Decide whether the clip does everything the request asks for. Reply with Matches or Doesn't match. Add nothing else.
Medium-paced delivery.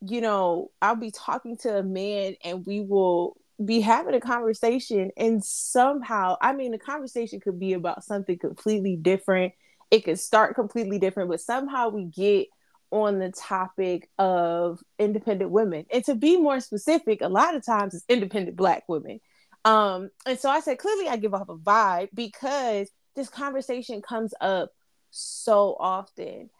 Matches